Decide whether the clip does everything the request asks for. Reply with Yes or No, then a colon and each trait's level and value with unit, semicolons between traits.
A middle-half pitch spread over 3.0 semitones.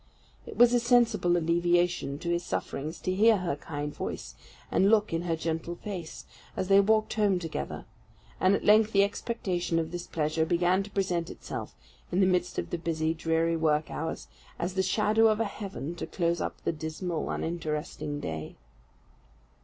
Yes: average, 3.5 semitones